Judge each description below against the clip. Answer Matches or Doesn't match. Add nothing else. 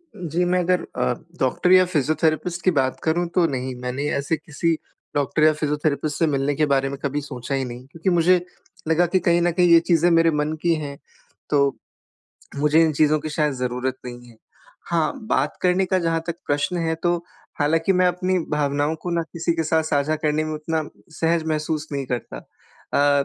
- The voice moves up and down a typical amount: Matches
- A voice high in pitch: Doesn't match